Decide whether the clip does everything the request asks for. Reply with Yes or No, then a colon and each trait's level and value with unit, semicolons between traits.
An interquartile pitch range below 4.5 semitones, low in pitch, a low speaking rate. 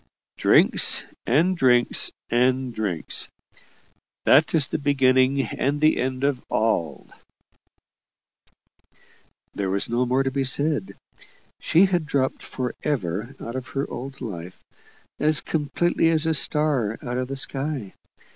Yes: average, 3.4 semitones; low, 130 Hz; slow, 130 wpm